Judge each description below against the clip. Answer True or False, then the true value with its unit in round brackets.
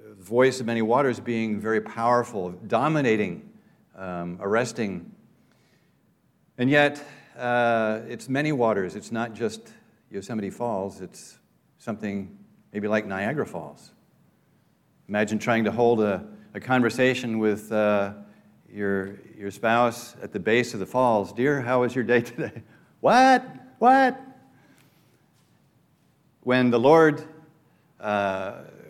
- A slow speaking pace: True (120 wpm)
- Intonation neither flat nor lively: True (3.6 semitones)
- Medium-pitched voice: False (115 Hz)